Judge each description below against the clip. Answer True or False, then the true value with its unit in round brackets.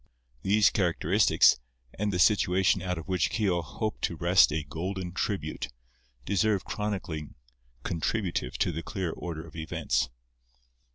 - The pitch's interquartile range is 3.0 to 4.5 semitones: True (3.4 semitones)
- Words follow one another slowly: True (130 wpm)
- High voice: False (90 Hz)